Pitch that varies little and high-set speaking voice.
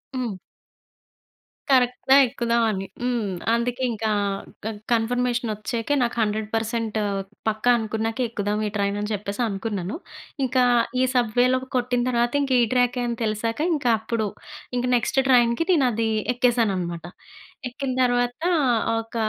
Yes: narrow, 2.3 semitones; high, 235 Hz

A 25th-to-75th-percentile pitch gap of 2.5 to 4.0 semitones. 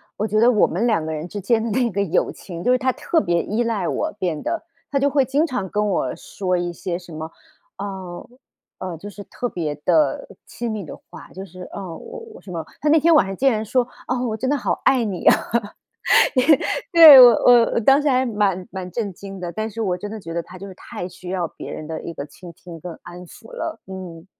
No: wide, 5.6 semitones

